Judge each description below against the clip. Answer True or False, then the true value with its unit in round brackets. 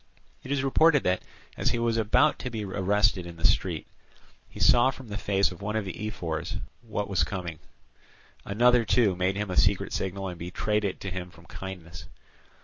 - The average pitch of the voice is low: True (100 Hz)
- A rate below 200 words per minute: False (205 wpm)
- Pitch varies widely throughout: False (3.4 semitones)